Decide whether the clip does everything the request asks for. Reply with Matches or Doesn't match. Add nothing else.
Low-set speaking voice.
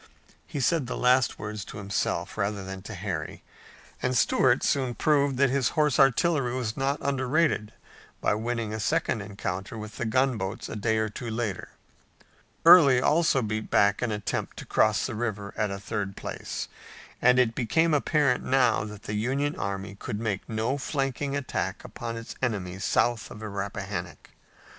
Matches